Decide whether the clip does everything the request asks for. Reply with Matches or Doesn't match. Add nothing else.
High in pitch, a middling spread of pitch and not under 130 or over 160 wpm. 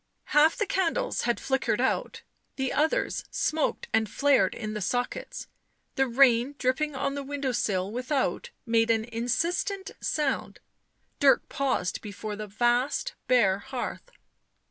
Matches